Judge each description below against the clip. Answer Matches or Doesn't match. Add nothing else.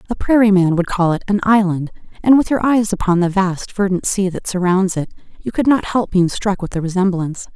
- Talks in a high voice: Matches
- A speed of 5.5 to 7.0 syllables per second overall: Matches